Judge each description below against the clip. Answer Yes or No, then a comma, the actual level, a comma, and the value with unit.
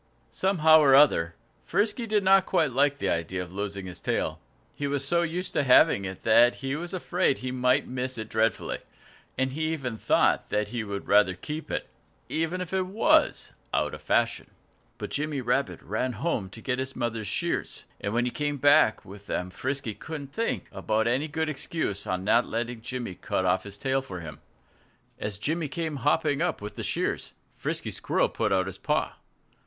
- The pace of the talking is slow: No, average, 190 wpm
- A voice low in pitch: Yes, low, 130 Hz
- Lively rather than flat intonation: Yes, wide, 6.8 semitones